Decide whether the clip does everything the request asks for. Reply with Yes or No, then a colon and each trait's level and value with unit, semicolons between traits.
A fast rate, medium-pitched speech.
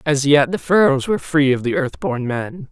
Yes: fast, 245 wpm; medium, 160 Hz